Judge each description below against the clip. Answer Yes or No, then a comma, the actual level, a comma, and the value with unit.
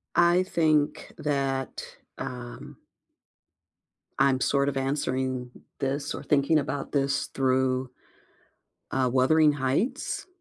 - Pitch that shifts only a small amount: Yes, narrow, 2.1 semitones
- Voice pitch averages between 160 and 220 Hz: No, low, 135 Hz